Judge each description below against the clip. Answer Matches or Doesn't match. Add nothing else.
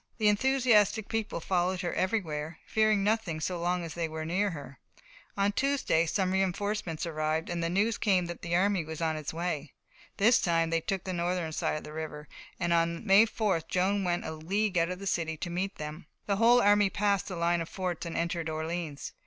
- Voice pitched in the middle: Matches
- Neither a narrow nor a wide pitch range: Matches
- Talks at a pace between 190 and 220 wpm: Matches